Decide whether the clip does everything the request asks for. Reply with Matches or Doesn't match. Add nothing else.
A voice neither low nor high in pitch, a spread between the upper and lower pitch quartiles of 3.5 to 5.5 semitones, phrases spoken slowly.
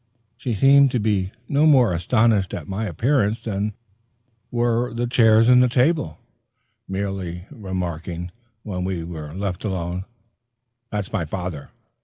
Doesn't match